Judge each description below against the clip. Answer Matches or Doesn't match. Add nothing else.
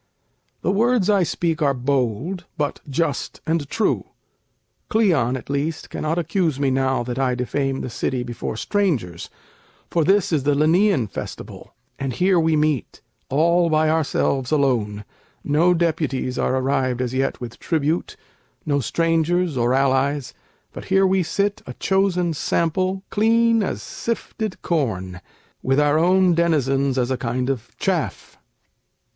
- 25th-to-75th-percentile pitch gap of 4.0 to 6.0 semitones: Matches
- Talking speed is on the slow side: Doesn't match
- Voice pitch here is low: Doesn't match